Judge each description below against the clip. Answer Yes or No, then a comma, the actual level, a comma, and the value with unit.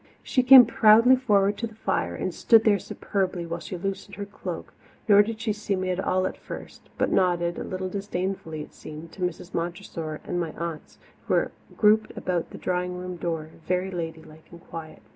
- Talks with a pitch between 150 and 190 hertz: Yes, medium, 185 Hz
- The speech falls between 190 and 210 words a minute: Yes, average, 200 wpm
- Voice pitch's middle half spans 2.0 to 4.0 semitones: Yes, average, 3.3 semitones